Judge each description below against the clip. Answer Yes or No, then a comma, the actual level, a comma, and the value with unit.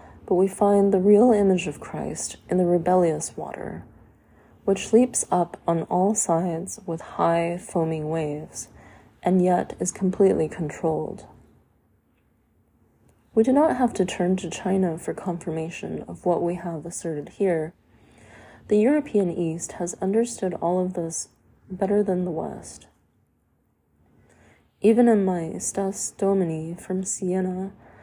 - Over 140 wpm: No, slow, 135 wpm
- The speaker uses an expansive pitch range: No, average, 2.9 semitones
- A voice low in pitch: No, medium, 180 Hz